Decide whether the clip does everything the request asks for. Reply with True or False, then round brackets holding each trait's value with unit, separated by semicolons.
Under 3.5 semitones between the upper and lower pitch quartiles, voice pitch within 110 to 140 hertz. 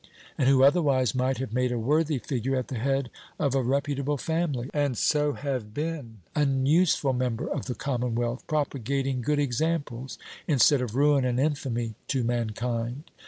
True (2.9 semitones; 135 Hz)